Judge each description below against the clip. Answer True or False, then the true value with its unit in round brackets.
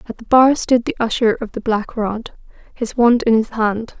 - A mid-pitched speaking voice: False (230 Hz)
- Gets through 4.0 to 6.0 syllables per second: True (4.7 syllables/s)